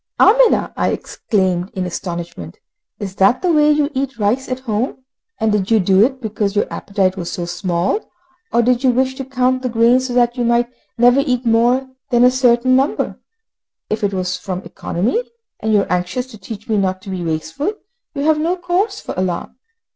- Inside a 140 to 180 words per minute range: No, average, 200 wpm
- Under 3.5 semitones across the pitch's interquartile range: No, wide, 5.4 semitones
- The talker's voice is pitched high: Yes, high, 235 Hz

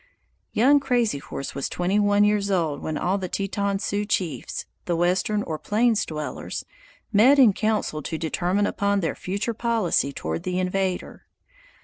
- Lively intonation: No, average, 3.5 semitones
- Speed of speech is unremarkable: Yes, average, 155 wpm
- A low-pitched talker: No, high, 195 Hz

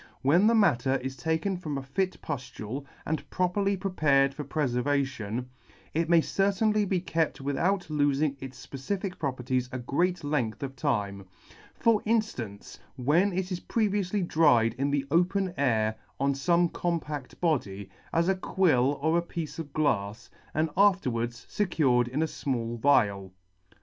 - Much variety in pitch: Yes, wide, 5.8 semitones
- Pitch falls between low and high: Yes, medium, 145 Hz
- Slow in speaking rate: No, average, 155 wpm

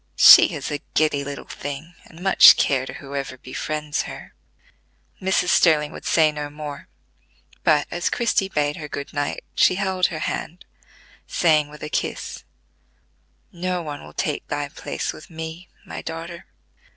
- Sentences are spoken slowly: No, average, 155 wpm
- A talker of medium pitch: Yes, medium, 155 Hz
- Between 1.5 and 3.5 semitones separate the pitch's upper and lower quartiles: Yes, average, 2.9 semitones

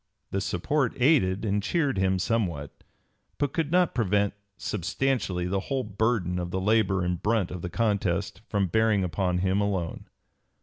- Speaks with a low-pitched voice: Yes, low, 100 Hz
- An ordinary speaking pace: Yes, average, 160 wpm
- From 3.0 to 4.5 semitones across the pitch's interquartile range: Yes, average, 4.0 semitones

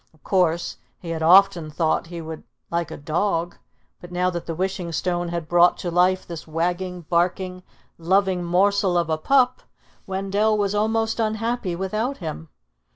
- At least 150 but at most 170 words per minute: Yes, average, 160 wpm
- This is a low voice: No, medium, 180 Hz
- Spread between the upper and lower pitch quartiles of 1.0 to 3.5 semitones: Yes, average, 2.7 semitones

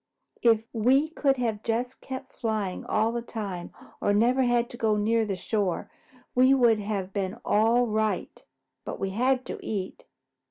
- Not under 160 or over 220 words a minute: Yes, average, 165 wpm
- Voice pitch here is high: Yes, high, 225 Hz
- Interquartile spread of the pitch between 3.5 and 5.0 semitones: No, average, 2.9 semitones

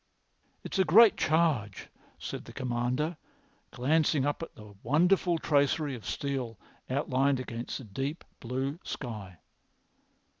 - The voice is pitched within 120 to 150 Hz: Yes, low, 135 Hz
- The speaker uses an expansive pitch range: No, average, 4.3 semitones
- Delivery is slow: Yes, slow, 120 wpm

